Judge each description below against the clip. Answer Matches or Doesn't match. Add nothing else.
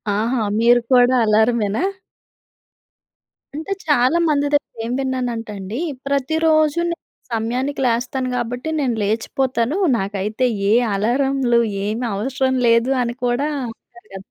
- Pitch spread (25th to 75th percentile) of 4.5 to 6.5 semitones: Doesn't match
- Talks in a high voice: Matches